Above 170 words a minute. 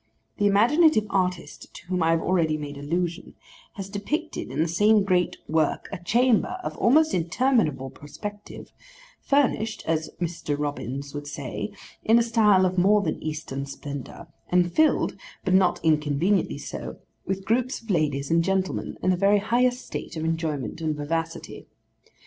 No: average, 155 wpm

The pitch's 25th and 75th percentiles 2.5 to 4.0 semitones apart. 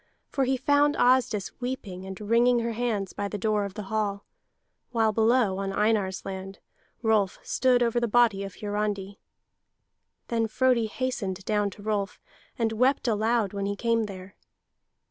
Yes: average, 3.2 semitones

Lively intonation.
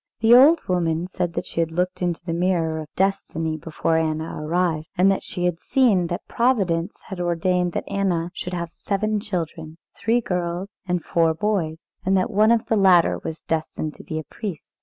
No: average, 3.0 semitones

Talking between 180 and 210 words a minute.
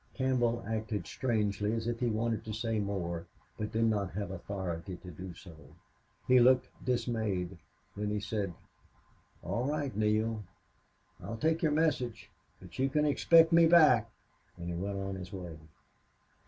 No: average, 155 wpm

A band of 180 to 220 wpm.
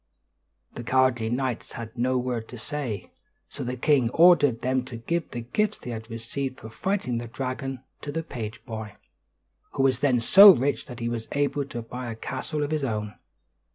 Yes: average, 190 wpm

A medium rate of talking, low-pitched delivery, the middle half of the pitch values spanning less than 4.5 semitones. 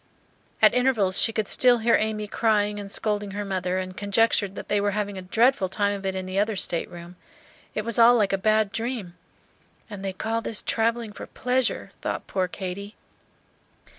No: average, 190 wpm; high, 205 Hz; average, 2.8 semitones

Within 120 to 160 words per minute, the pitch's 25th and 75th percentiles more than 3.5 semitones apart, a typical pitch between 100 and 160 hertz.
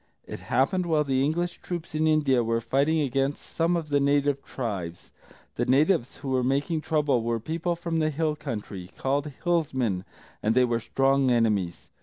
No: average, 175 wpm; average, 4.5 semitones; medium, 140 Hz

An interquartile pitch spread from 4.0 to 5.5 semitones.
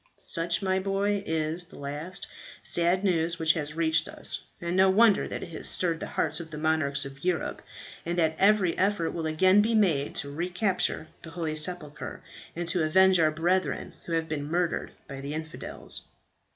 No: average, 3.0 semitones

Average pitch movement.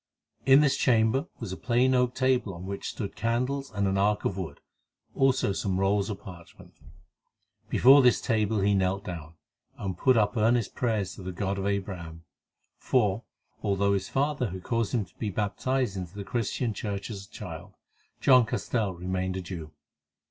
Yes: average, 4.3 semitones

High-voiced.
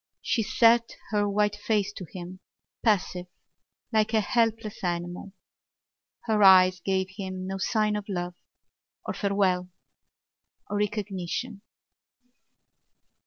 Yes: high, 200 Hz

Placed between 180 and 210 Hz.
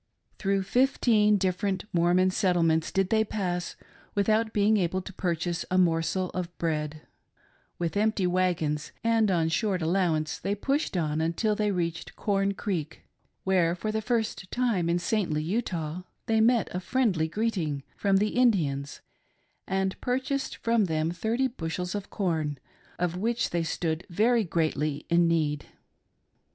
Yes: medium, 185 Hz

